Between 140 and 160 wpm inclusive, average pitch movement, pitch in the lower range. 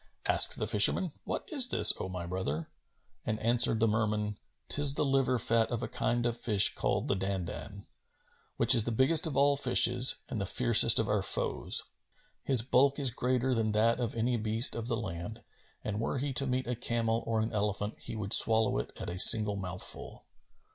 No: average, 195 wpm; average, 3.1 semitones; low, 115 Hz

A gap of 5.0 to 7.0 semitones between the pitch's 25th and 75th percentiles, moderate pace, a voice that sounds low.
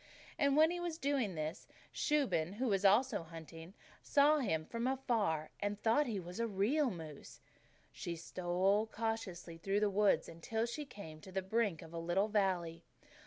No: wide, 5.5 semitones; average, 175 wpm; high, 200 Hz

